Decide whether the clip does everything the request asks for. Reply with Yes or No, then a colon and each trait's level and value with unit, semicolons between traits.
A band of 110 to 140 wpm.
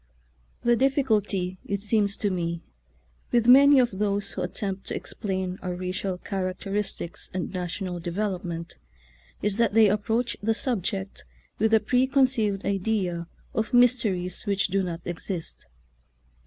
Yes: slow, 135 wpm